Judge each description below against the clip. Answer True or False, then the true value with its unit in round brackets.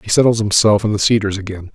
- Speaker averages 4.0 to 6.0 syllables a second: False (6.4 syllables/s)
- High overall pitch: False (105 Hz)